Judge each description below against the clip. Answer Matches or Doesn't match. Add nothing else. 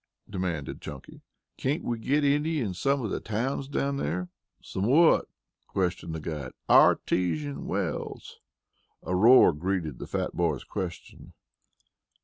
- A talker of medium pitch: Doesn't match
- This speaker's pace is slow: Matches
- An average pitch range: Doesn't match